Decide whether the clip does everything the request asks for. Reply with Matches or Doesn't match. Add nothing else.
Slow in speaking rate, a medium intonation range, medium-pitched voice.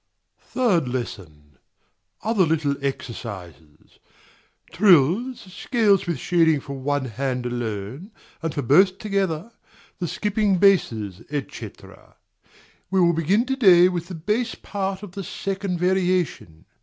Doesn't match